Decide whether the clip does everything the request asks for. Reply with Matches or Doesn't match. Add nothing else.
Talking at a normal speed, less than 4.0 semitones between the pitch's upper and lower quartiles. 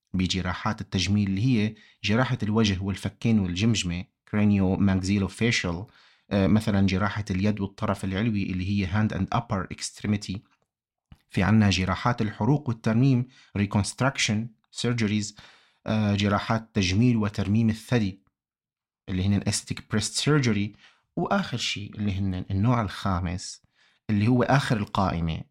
Matches